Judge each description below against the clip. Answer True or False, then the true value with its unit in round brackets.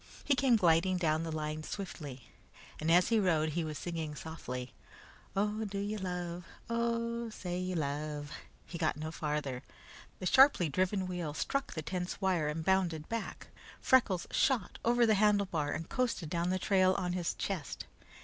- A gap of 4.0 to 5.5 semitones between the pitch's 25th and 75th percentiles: True (4.4 semitones)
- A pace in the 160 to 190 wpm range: True (170 wpm)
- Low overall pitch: False (180 Hz)